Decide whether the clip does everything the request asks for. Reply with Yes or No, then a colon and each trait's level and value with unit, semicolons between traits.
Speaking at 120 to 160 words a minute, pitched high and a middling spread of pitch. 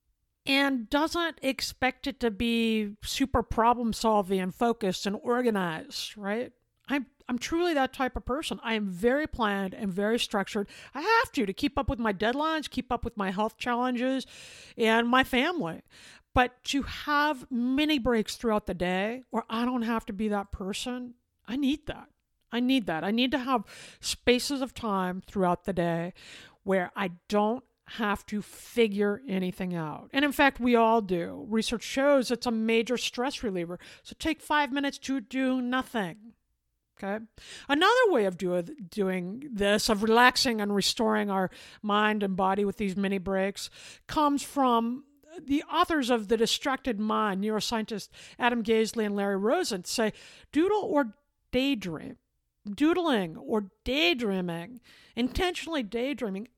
Yes: average, 155 wpm; high, 235 Hz; average, 4.5 semitones